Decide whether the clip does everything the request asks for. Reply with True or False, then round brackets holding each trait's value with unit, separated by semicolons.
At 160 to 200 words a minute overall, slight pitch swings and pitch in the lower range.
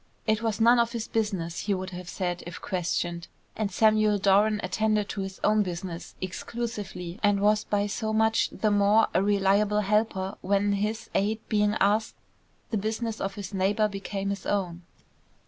False (170 wpm; 2.1 semitones; 205 Hz)